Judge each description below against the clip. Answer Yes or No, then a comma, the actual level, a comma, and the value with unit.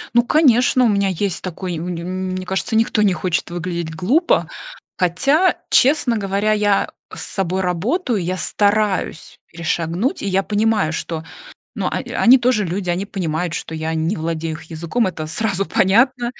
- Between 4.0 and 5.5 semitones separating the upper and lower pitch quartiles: Yes, average, 4.6 semitones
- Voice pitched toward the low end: No, high, 190 Hz